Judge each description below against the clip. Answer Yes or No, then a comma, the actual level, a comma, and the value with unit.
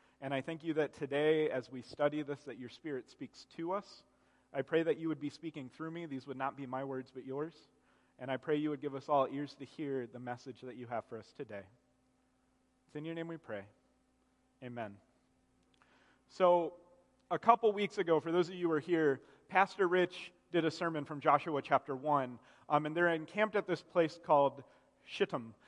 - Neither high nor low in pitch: Yes, medium, 145 Hz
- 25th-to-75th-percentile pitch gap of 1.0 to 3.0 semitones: No, average, 3.8 semitones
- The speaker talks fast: Yes, fast, 210 wpm